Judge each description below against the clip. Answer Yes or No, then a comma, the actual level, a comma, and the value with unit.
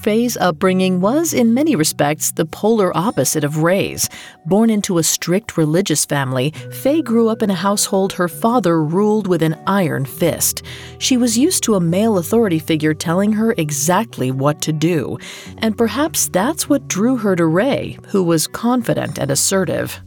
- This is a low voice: No, medium, 185 Hz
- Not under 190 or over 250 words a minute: No, average, 170 wpm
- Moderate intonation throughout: No, wide, 5.7 semitones